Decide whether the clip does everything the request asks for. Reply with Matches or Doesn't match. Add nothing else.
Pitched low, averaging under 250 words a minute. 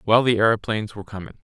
Matches